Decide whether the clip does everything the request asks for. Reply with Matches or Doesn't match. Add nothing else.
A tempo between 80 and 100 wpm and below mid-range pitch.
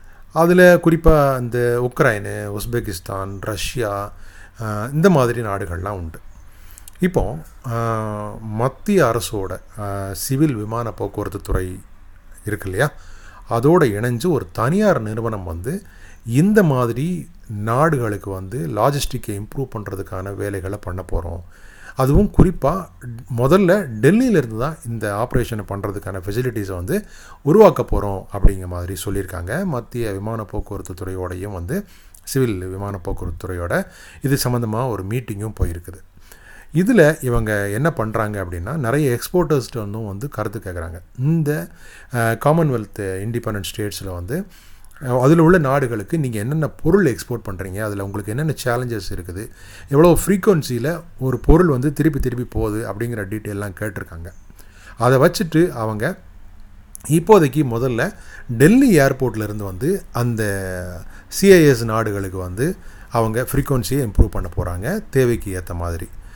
Doesn't match